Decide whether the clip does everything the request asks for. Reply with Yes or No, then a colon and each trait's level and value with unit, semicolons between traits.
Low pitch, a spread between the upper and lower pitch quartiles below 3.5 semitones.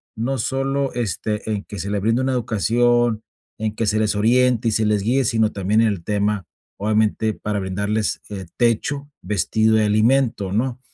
Yes: low, 110 Hz; narrow, 2.6 semitones